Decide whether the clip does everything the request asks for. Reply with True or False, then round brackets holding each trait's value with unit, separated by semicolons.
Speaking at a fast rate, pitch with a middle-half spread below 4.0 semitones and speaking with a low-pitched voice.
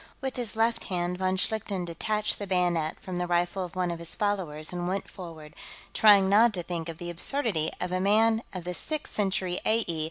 False (210 wpm; 3.3 semitones; 185 Hz)